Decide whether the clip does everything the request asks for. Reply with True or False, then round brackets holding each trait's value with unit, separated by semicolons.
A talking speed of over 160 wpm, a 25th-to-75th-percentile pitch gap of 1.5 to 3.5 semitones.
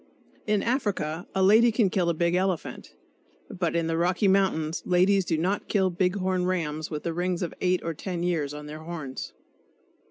True (190 wpm; 2.6 semitones)